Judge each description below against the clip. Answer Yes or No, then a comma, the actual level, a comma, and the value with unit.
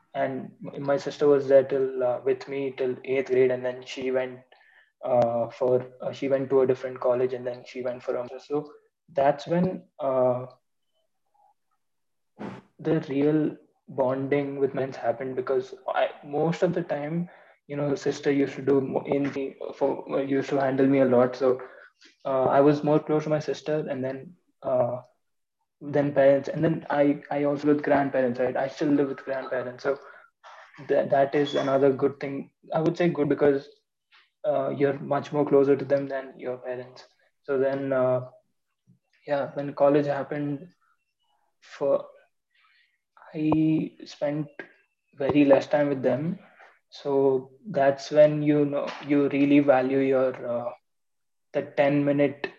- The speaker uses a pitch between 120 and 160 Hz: Yes, medium, 140 Hz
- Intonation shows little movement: Yes, narrow, 2.2 semitones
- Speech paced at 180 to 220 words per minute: No, average, 160 wpm